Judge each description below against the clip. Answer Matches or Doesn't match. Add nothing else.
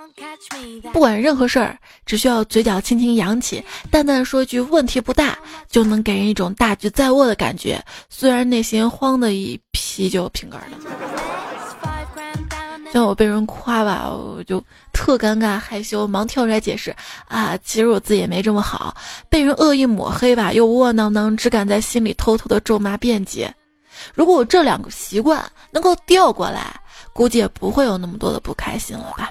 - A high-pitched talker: Matches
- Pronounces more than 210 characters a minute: Matches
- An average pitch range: Matches